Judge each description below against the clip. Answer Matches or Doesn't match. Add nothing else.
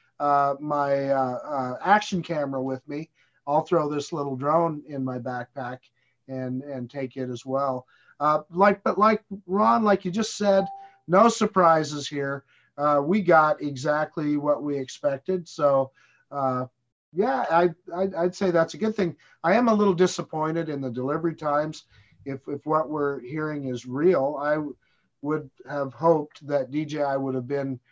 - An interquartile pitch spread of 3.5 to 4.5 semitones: Matches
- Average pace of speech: Matches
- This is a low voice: Doesn't match